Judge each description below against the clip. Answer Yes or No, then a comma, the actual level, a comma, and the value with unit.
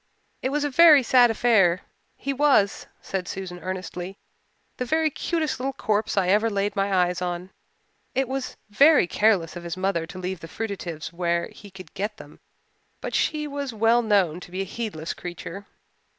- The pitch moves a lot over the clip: Yes, wide, 5.7 semitones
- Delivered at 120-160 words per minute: No, average, 180 wpm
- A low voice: No, high, 200 Hz